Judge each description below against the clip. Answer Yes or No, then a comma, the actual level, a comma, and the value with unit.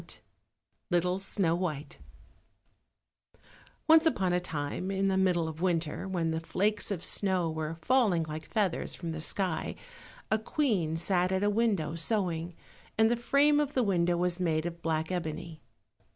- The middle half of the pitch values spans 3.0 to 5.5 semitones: Yes, average, 3.7 semitones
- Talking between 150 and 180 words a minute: Yes, average, 160 wpm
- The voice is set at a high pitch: No, medium, 180 Hz